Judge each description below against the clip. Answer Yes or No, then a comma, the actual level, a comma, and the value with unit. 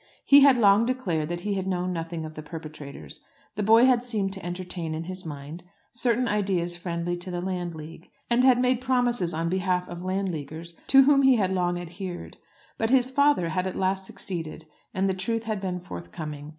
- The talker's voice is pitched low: No, medium, 185 Hz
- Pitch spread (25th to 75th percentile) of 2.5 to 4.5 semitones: No, average, 4.9 semitones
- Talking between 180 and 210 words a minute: Yes, average, 190 wpm